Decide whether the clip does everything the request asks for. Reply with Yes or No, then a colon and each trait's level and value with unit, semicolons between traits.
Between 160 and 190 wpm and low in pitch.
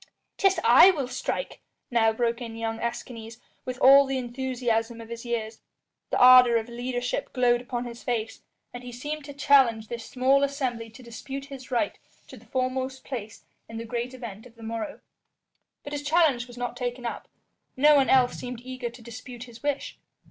No: average, 185 wpm; high, 245 Hz